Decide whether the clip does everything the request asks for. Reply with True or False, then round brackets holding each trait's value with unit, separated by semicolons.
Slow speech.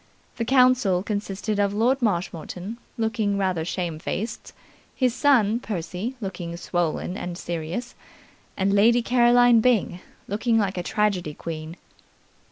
True (120 wpm)